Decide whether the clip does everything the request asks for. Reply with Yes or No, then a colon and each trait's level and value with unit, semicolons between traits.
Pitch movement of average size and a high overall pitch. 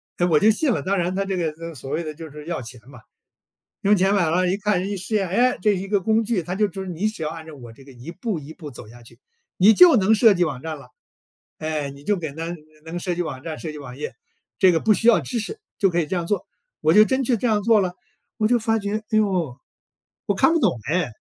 No: average, 5.0 semitones; medium, 180 Hz